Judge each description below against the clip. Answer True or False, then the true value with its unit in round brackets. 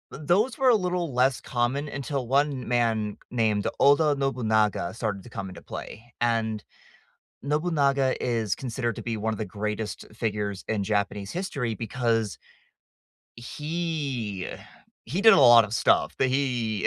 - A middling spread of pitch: True (4.5 semitones)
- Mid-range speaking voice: False (120 Hz)